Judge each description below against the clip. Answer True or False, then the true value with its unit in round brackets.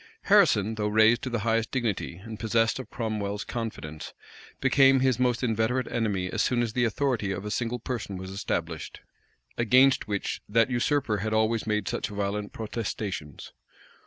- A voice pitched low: True (110 Hz)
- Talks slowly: False (160 wpm)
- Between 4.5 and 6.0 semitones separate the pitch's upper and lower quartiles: False (2.8 semitones)